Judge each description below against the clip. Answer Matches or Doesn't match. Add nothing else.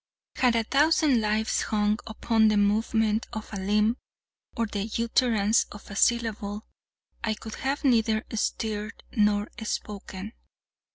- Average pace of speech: Doesn't match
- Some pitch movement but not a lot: Doesn't match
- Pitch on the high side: Matches